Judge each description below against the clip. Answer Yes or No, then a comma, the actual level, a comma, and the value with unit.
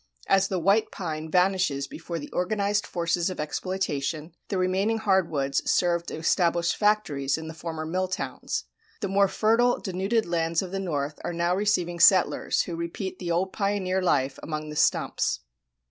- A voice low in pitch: No, medium, 180 Hz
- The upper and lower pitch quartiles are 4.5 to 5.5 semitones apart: No, average, 3.2 semitones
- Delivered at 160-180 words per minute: Yes, average, 170 wpm